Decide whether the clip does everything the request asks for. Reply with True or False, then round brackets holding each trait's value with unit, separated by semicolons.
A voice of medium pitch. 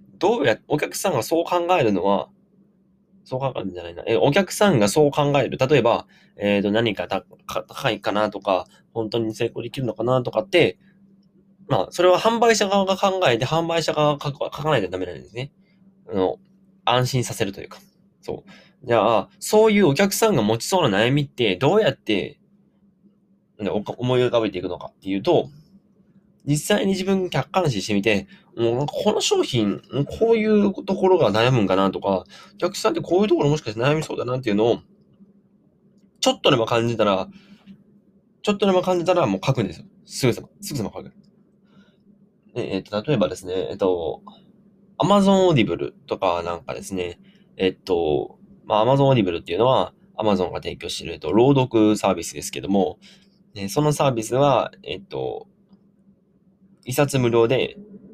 True (180 Hz)